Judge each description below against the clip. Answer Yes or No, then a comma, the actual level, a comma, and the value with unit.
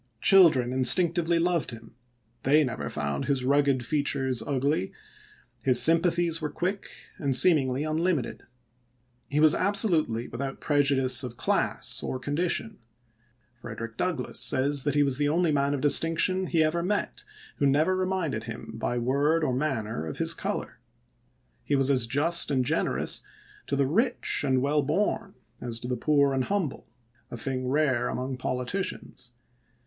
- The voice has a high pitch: No, medium, 140 Hz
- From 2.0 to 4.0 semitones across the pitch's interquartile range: No, average, 4.4 semitones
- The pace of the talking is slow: No, average, 155 wpm